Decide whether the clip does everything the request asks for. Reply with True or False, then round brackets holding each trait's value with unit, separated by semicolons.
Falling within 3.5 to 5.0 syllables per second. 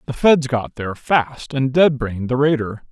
True (4.8 syllables/s)